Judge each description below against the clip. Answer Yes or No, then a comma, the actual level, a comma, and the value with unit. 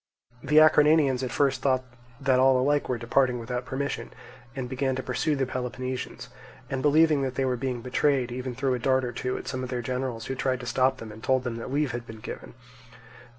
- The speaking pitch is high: No, low, 130 Hz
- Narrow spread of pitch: Yes, narrow, 1.5 semitones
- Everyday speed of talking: No, fast, 220 wpm